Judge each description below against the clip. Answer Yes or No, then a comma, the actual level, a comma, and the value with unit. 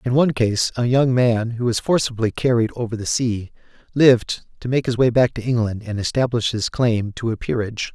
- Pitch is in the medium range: No, low, 120 Hz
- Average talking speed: No, fast, 210 wpm